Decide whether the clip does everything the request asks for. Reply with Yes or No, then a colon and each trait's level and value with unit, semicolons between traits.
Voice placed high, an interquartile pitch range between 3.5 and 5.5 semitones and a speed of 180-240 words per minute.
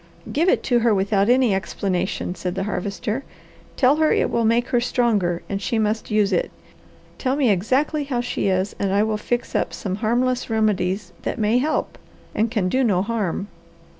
Yes: high, 220 Hz; average, 3.9 semitones; average, 190 wpm